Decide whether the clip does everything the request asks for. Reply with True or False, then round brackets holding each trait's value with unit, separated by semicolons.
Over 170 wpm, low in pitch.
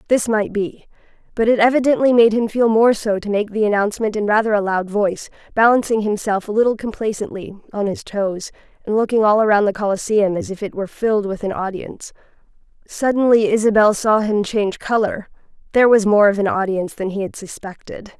False (190 wpm; 210 Hz)